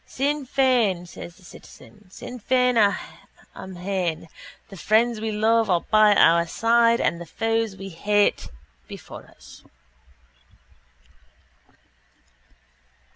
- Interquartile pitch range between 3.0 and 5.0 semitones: Yes, average, 4.1 semitones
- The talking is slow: Yes, slow, 105 wpm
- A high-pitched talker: Yes, high, 215 Hz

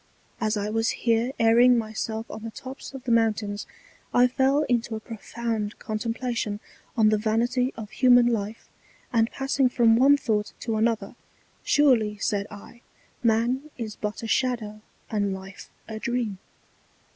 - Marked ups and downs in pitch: No, narrow, 2.4 semitones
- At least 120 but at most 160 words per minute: Yes, average, 155 wpm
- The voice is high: Yes, high, 225 Hz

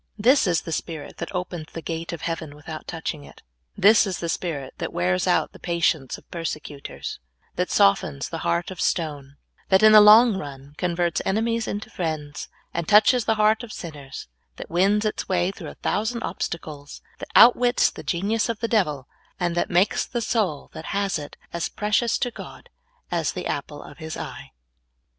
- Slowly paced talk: No, average, 185 wpm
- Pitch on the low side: No, medium, 175 Hz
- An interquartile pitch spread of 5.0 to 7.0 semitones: Yes, wide, 5.4 semitones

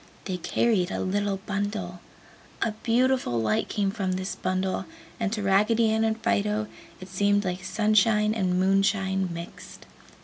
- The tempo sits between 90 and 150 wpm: Yes, average, 145 wpm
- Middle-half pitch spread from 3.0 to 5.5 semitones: No, narrow, 2.5 semitones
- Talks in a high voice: Yes, high, 200 Hz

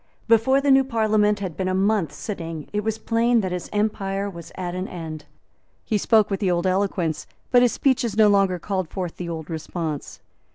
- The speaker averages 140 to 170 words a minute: No, average, 200 wpm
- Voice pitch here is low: No, high, 195 Hz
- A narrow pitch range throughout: No, average, 3.8 semitones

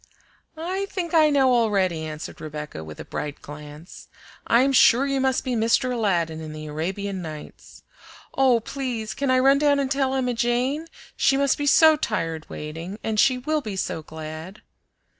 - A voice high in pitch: Yes, high, 230 Hz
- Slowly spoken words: No, average, 175 wpm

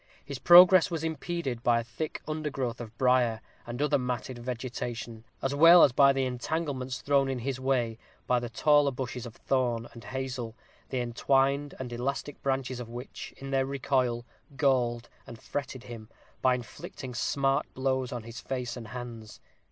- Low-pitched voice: Yes, low, 130 Hz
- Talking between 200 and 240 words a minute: No, average, 165 wpm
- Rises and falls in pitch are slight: Yes, narrow, 2.3 semitones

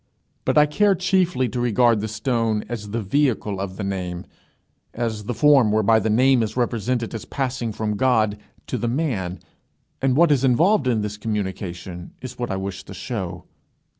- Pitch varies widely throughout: No, average, 4.0 semitones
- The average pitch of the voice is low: Yes, low, 115 Hz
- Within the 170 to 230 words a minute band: Yes, average, 180 wpm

